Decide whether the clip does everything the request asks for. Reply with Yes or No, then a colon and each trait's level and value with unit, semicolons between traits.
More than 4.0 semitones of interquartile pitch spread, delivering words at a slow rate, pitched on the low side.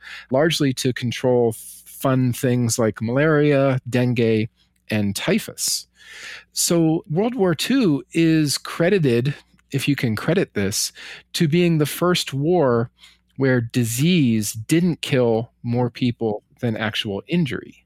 Yes: wide, 5.6 semitones; slow, 120 wpm; low, 130 Hz